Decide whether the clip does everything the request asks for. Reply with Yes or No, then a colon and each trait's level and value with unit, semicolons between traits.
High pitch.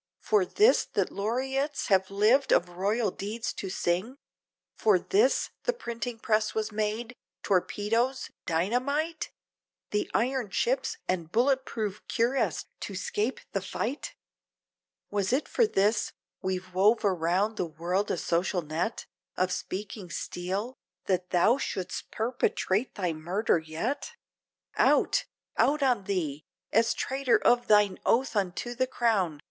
Yes: high, 210 Hz